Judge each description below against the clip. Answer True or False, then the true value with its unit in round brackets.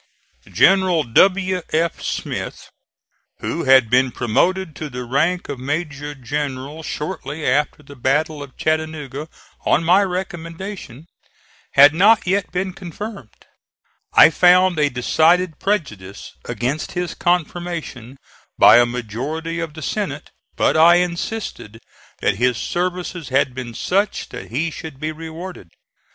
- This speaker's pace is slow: True (130 wpm)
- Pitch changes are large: False (4.9 semitones)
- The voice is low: False (155 Hz)